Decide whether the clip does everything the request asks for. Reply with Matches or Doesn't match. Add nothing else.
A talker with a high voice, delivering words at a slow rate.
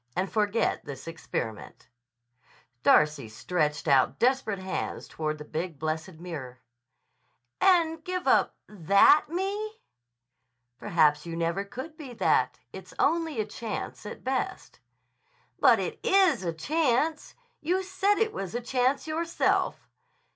Matches